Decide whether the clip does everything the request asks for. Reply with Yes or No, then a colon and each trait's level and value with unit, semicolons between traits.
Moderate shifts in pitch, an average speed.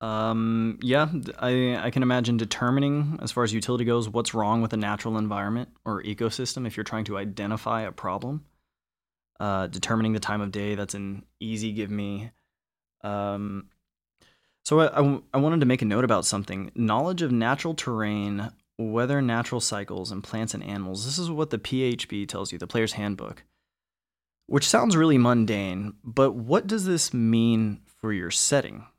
Yes: average, 3.5 semitones; average, 175 wpm